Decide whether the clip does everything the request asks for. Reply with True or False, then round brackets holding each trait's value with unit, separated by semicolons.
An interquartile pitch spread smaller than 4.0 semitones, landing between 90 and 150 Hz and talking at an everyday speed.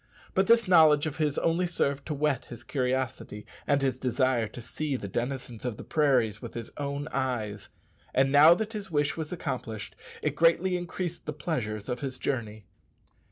False (4.4 semitones; 140 Hz; 180 wpm)